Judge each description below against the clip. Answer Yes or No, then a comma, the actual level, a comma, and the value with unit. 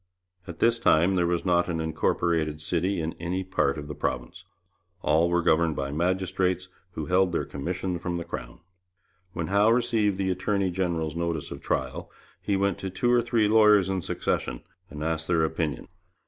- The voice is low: Yes, very low, 85 Hz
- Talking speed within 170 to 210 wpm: Yes, average, 180 wpm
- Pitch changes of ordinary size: Yes, average, 3.0 semitones